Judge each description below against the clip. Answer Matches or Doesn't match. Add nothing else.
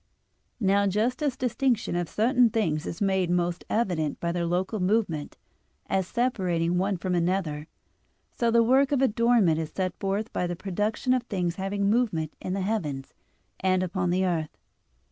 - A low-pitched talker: Doesn't match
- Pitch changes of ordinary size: Matches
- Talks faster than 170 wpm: Doesn't match